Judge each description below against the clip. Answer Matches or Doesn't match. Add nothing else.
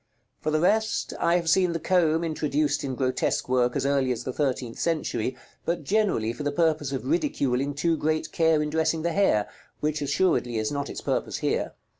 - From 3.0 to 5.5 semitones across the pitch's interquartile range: Matches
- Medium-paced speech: Matches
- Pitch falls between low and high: Matches